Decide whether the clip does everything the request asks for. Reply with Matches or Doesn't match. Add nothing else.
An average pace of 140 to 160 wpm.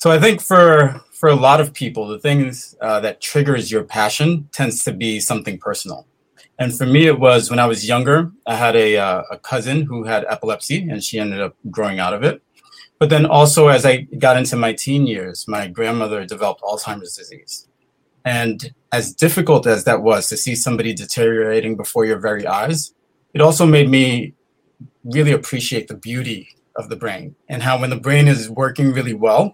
Doesn't match